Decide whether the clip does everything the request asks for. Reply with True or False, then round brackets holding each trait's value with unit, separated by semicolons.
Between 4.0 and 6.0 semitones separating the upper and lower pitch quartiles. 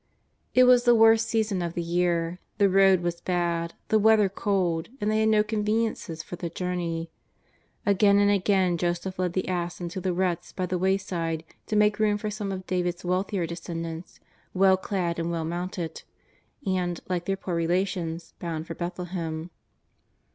False (2.8 semitones)